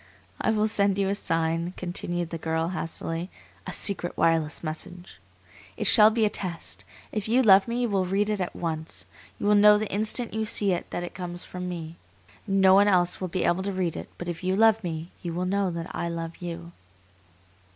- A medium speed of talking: No, fast, 215 wpm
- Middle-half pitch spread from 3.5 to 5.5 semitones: No, average, 3.1 semitones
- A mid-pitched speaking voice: Yes, medium, 180 Hz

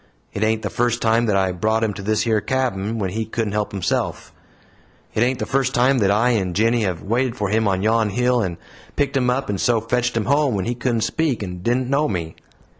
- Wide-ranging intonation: No, average, 3.4 semitones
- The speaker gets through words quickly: Yes, fast, 240 wpm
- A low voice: Yes, low, 115 Hz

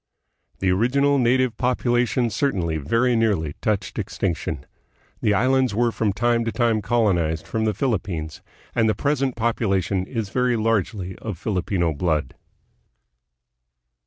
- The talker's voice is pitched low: Yes, low, 110 Hz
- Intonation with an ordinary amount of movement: Yes, average, 4.4 semitones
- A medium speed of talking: No, slow, 130 wpm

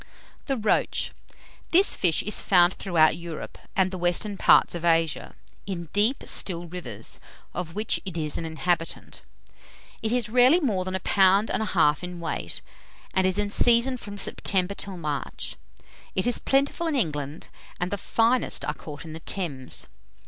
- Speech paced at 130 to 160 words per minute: No, average, 170 wpm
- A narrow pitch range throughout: No, average, 4.4 semitones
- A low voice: No, medium, 185 Hz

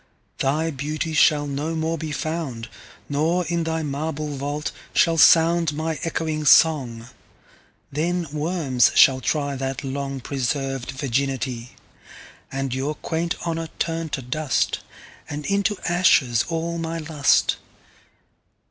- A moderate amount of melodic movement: Yes, average, 3.2 semitones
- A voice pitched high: No, medium, 150 Hz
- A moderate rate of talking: No, slow, 105 wpm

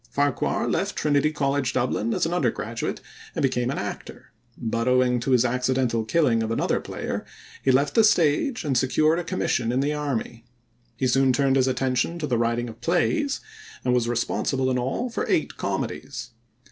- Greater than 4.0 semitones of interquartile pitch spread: No, average, 3.3 semitones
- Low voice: Yes, low, 130 Hz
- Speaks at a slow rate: No, average, 180 wpm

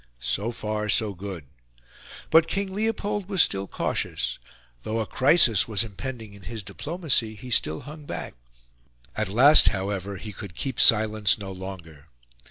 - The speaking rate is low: No, average, 150 wpm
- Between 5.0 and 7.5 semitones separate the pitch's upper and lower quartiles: Yes, wide, 5.6 semitones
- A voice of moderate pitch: No, low, 110 Hz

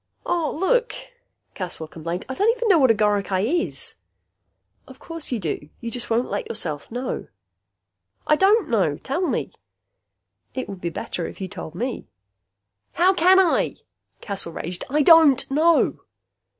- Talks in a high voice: Yes, very high, 250 Hz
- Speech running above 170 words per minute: No, average, 155 wpm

